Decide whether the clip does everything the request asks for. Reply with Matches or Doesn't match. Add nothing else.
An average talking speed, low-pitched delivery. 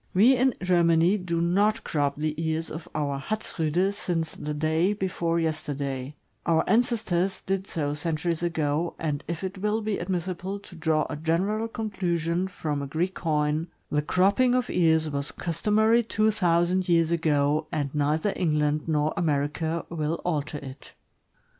Doesn't match